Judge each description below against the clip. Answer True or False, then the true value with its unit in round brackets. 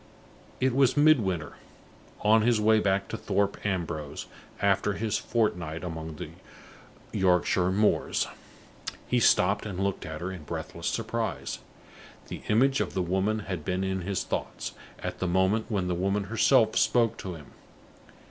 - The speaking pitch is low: True (100 Hz)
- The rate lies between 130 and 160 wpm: True (150 wpm)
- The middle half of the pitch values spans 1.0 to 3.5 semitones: True (3.2 semitones)